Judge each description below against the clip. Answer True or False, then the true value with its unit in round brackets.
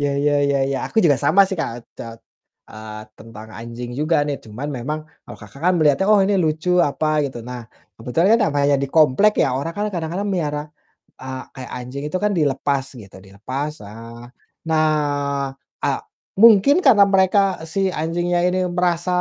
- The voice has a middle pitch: True (145 Hz)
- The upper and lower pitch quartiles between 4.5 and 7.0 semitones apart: True (5.6 semitones)